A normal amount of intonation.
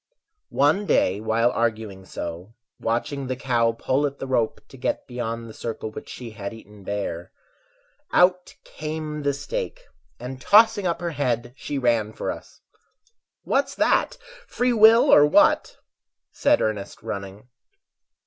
No: wide, 5.7 semitones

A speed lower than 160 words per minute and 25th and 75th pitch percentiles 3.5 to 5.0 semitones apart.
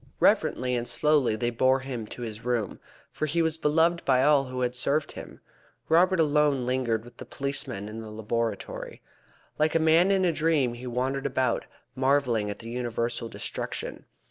No: average, 175 wpm; average, 4.2 semitones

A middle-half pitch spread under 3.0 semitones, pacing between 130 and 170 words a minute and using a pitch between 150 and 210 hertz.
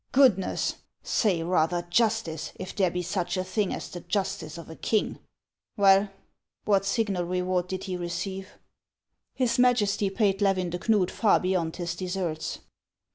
Yes: narrow, 2.5 semitones; average, 160 wpm; medium, 185 Hz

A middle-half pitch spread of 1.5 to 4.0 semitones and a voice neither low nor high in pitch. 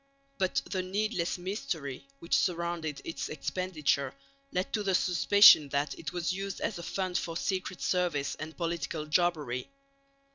Yes: average, 3.3 semitones; medium, 170 Hz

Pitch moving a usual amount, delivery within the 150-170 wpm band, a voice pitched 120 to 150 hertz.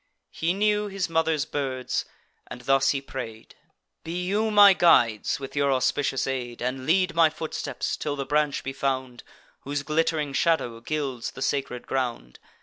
Yes: average, 3.8 semitones; average, 155 wpm; medium, 140 Hz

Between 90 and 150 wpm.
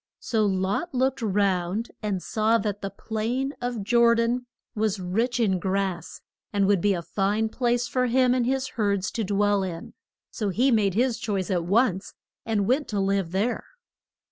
No: average, 175 wpm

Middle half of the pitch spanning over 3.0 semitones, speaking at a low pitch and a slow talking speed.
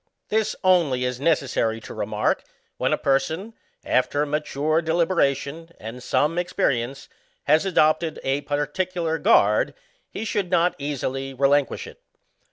No: average, 3.8 semitones; medium, 150 Hz; slow, 130 wpm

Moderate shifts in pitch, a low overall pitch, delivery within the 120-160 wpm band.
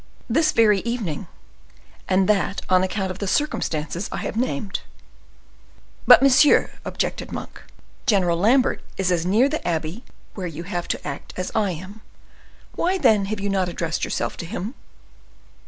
No: average, 4.3 semitones; high, 195 Hz; average, 155 wpm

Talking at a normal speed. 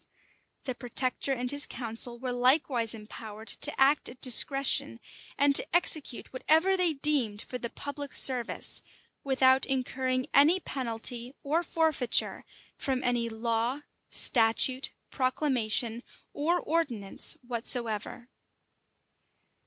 No: slow, 110 wpm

